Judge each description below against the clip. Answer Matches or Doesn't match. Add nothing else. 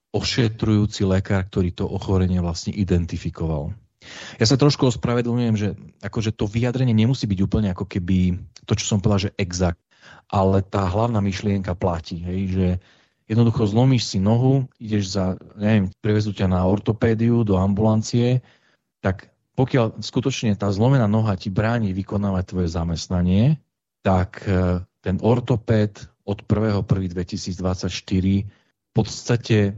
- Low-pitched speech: Matches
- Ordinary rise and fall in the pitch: Matches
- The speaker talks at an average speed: Matches